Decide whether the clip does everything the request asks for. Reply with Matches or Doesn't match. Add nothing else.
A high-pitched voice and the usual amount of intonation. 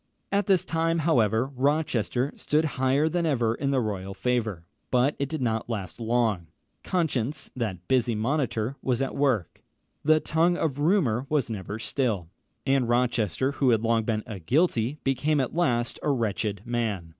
Doesn't match